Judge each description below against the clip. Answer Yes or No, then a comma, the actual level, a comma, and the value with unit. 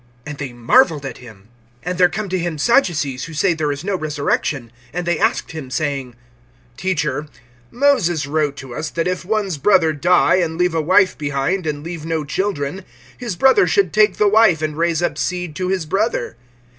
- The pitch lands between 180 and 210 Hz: No, medium, 165 Hz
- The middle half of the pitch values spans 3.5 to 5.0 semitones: Yes, average, 4.3 semitones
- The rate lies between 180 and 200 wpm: Yes, average, 195 wpm